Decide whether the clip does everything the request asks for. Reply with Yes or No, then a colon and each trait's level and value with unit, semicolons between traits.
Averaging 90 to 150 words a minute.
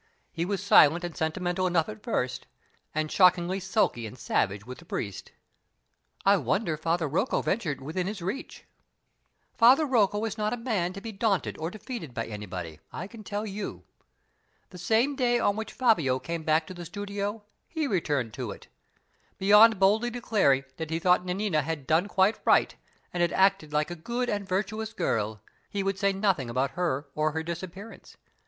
No: average, 180 wpm